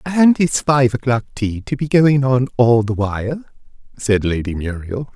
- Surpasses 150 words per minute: Yes, average, 175 wpm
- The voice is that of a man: Yes, male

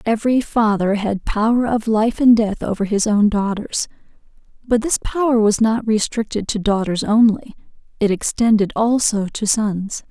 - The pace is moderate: Yes, average, 155 wpm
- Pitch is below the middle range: No, high, 215 Hz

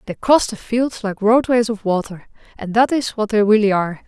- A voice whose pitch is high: Yes, high, 220 Hz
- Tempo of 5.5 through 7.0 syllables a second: No, 5.3 syllables/s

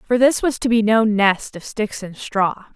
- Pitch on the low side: No, high, 220 Hz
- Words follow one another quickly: Yes, fast, 240 wpm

